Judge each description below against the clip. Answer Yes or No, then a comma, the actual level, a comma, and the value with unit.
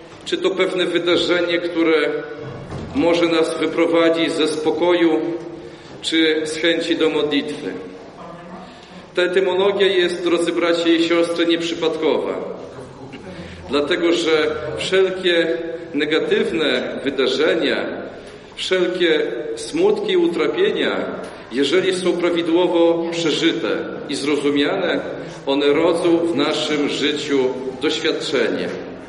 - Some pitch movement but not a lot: No, narrow, 2.1 semitones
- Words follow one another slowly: Yes, slow, 90 wpm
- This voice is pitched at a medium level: Yes, medium, 170 Hz